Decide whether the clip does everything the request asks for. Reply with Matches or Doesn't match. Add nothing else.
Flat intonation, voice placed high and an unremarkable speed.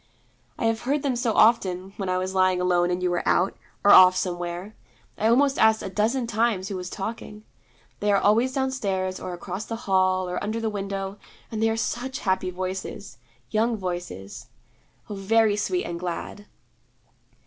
Doesn't match